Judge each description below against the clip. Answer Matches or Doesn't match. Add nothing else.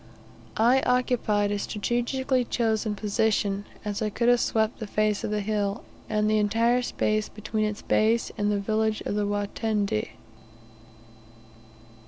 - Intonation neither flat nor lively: Doesn't match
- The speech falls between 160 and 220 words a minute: Doesn't match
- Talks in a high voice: Matches